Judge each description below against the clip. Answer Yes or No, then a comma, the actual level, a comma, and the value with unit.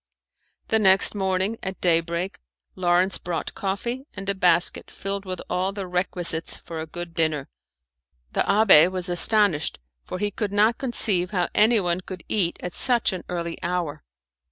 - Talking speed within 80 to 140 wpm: No, average, 160 wpm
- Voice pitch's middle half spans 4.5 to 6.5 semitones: No, narrow, 2.5 semitones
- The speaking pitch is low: No, medium, 185 Hz